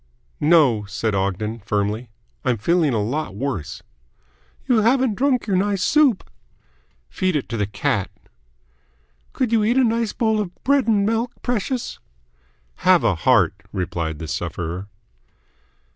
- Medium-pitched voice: Yes, medium, 155 Hz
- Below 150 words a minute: Yes, average, 140 wpm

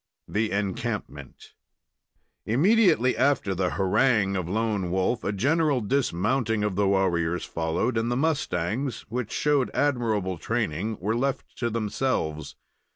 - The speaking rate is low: Yes, slow, 125 wpm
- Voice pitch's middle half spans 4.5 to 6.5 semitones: Yes, wide, 5.5 semitones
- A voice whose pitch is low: Yes, low, 110 Hz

